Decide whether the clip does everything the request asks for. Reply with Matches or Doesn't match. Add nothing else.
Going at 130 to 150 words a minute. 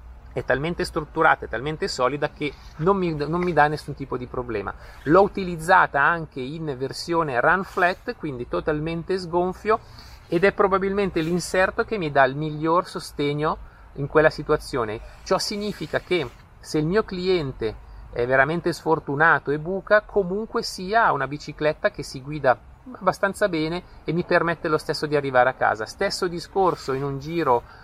Doesn't match